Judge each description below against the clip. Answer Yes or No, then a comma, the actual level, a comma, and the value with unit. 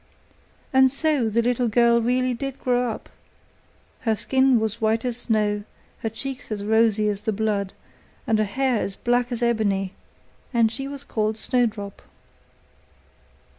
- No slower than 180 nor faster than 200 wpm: No, average, 155 wpm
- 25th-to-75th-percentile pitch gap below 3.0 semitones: Yes, narrow, 2.6 semitones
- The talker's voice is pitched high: Yes, high, 230 Hz